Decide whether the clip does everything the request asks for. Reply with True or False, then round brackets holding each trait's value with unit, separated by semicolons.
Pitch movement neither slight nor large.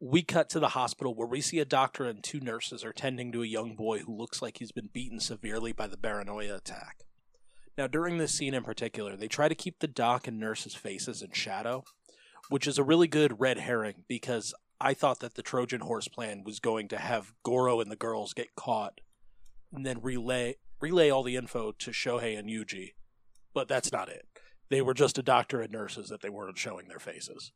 True (3.6 semitones)